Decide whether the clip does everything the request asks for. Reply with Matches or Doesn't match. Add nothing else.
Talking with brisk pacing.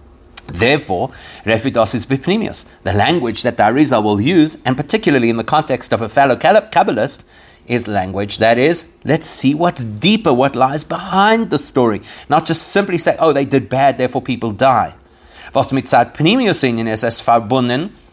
Doesn't match